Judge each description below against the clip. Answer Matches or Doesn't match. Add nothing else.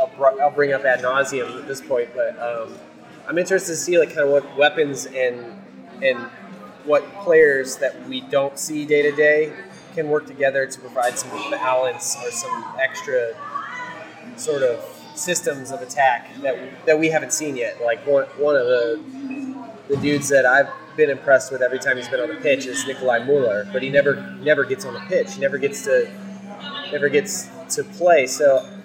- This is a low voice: Doesn't match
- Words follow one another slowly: Doesn't match